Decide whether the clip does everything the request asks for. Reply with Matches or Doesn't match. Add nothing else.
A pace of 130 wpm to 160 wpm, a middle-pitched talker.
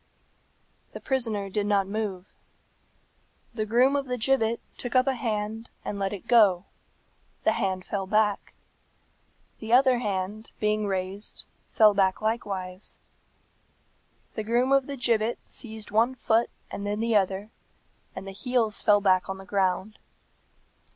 Doesn't match